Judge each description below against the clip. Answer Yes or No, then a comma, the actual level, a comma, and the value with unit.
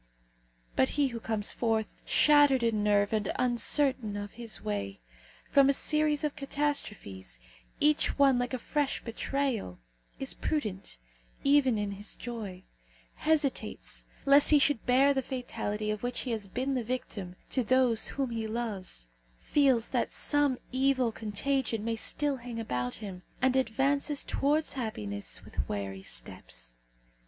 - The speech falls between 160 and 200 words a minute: No, average, 145 wpm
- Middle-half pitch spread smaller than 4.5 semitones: No, average, 4.9 semitones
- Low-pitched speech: No, high, 240 Hz